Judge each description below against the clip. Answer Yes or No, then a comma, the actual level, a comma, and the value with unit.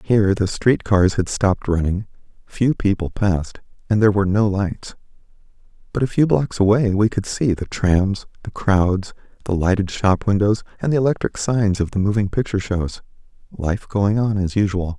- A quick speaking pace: No, average, 175 wpm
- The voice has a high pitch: No, low, 100 Hz